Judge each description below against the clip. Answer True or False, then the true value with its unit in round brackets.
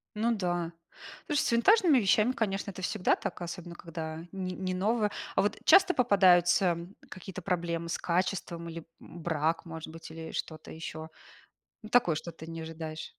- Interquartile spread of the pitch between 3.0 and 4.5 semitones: True (3.5 semitones)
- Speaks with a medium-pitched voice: True (175 Hz)